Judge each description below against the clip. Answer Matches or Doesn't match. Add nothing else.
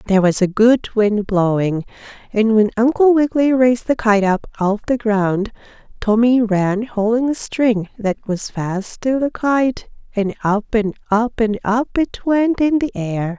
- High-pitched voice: Matches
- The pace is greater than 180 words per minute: Doesn't match